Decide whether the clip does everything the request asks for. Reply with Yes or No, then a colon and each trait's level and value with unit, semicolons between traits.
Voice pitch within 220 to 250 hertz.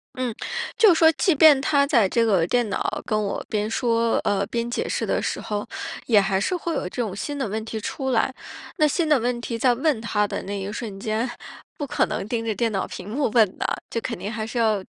Yes: high, 230 Hz